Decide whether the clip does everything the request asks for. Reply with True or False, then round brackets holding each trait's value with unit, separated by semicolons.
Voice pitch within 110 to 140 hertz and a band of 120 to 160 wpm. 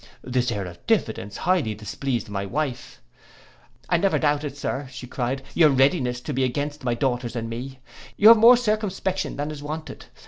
False (135 Hz; 175 wpm)